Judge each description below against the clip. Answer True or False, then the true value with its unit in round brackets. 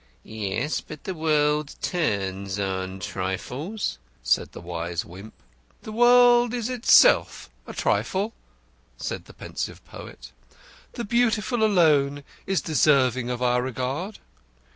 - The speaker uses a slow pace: True (120 wpm)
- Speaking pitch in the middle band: True (145 Hz)